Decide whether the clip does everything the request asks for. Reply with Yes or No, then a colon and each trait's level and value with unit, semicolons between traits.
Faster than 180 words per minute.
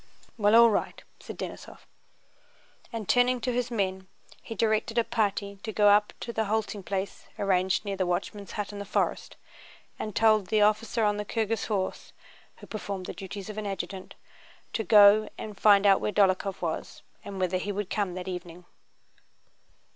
No: average, 175 wpm